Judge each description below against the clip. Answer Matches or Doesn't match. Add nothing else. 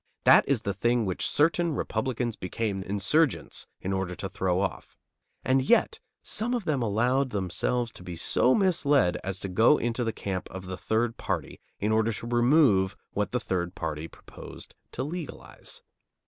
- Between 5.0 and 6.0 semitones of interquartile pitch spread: Matches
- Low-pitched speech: Matches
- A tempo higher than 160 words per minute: Matches